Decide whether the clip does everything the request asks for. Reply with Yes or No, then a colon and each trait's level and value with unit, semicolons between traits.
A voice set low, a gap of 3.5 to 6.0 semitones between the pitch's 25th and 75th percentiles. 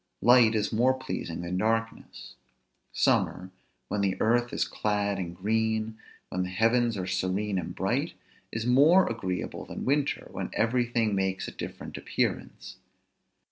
Yes: low, 110 Hz; average, 4.0 semitones